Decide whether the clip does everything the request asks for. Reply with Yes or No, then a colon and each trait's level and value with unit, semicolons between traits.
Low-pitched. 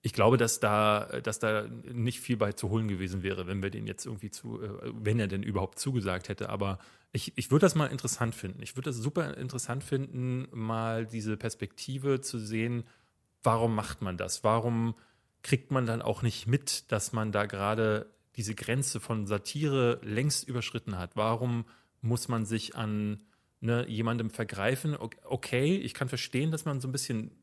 Yes: low, 115 Hz